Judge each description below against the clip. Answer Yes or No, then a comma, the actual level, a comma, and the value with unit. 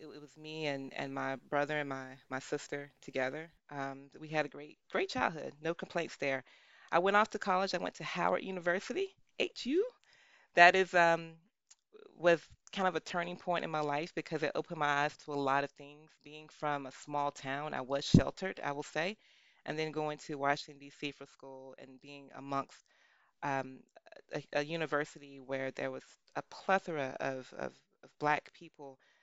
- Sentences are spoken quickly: No, average, 190 wpm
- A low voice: No, medium, 150 Hz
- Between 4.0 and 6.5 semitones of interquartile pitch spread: No, average, 3.5 semitones